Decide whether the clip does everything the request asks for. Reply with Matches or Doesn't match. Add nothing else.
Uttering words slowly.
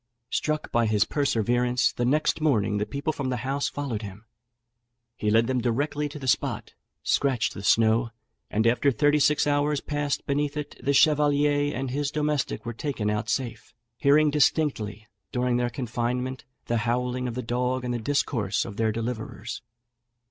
Doesn't match